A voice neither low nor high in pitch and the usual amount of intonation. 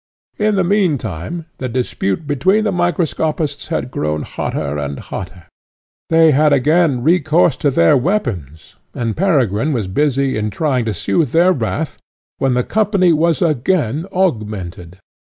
No: medium, 145 Hz; wide, 7.6 semitones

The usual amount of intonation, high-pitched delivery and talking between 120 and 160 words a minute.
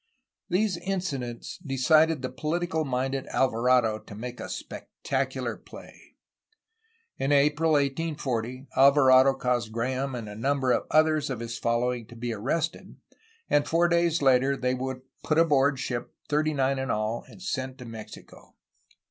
No: average, 3.6 semitones; low, 135 Hz; average, 145 wpm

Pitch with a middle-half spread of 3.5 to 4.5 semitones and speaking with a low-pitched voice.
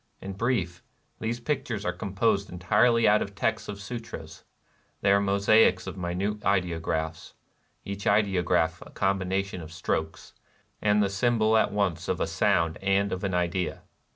No: average, 2.8 semitones; low, 100 Hz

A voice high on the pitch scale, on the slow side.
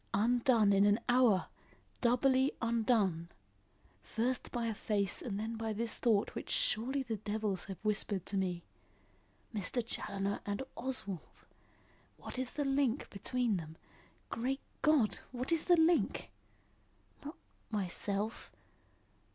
Yes: high, 225 Hz; slow, 125 wpm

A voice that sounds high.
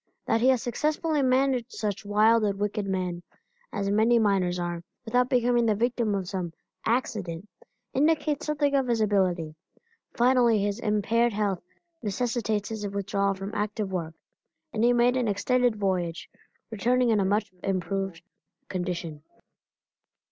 Yes: high, 210 Hz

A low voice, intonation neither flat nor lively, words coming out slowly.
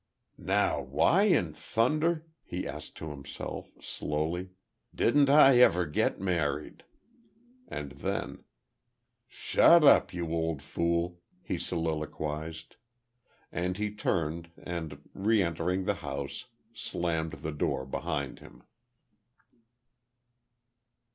Yes: very low, 85 Hz; average, 4.2 semitones; slow, 100 wpm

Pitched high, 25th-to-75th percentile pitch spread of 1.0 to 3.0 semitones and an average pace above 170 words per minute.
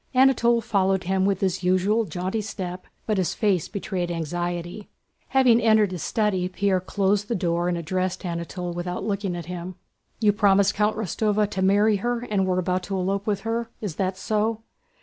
Yes: high, 195 Hz; average, 2.7 semitones; average, 180 wpm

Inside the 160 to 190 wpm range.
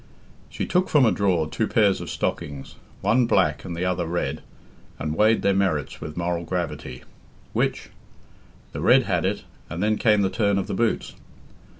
Yes: average, 180 wpm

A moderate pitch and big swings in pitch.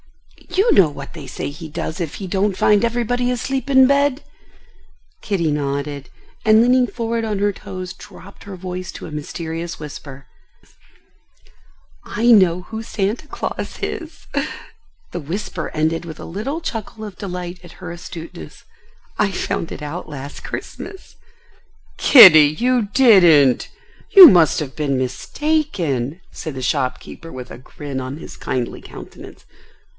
Yes: medium, 180 Hz; wide, 7.1 semitones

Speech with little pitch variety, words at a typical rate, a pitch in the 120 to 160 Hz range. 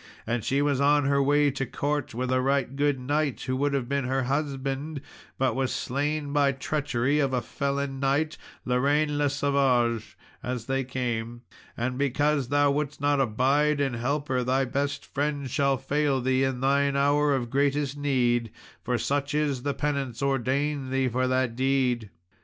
Yes: narrow, 1.9 semitones; average, 175 wpm; low, 135 Hz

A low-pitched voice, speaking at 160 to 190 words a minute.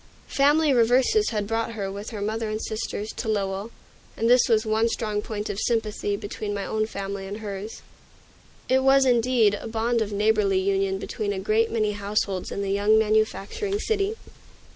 No: high, 215 Hz; average, 180 wpm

